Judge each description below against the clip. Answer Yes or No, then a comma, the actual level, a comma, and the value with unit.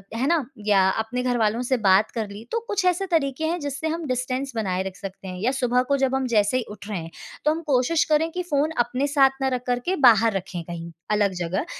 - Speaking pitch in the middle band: No, very high, 250 Hz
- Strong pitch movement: Yes, wide, 5.8 semitones